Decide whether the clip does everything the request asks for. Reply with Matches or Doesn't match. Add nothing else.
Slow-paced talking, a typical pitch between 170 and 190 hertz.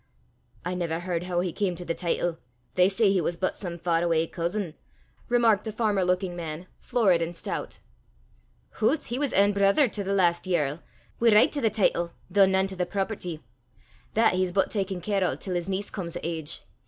Doesn't match